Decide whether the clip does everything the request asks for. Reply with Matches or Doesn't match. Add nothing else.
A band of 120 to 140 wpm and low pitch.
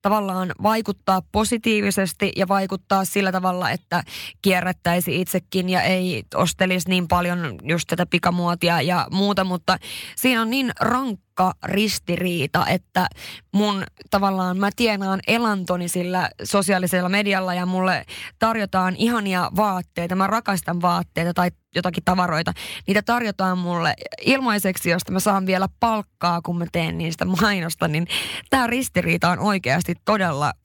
Doesn't match